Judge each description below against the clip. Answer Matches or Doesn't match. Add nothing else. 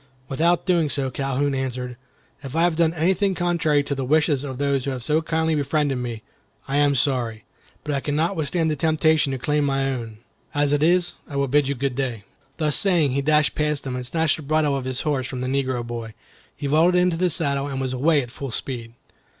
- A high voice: Doesn't match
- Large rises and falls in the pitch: Doesn't match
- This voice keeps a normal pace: Doesn't match